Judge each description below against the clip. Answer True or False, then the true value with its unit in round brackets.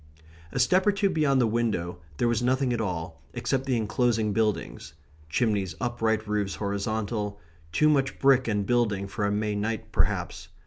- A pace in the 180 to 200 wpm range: False (170 wpm)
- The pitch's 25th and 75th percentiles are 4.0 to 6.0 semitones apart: False (3.4 semitones)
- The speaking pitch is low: True (110 Hz)